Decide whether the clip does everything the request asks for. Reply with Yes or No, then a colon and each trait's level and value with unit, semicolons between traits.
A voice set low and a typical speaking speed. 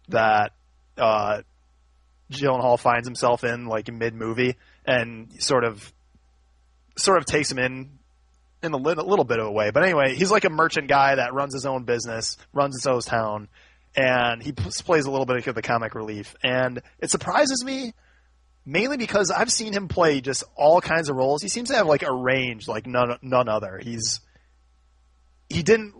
Yes: low, 125 Hz; average, 185 wpm